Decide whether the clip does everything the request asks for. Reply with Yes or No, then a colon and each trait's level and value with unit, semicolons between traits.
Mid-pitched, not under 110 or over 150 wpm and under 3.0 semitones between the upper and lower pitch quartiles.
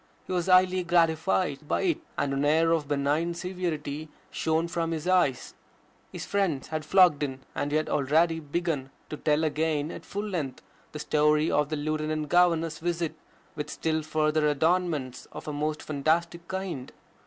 No: medium, 155 Hz; average, 165 wpm; narrow, 2.4 semitones